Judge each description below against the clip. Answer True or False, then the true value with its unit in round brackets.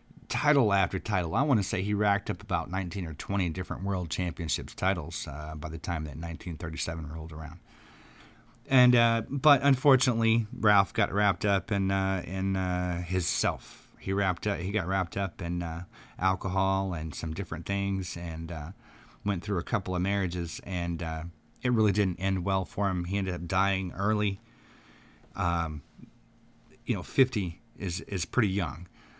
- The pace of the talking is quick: False (175 wpm)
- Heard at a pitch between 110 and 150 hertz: False (95 Hz)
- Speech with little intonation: False (3.3 semitones)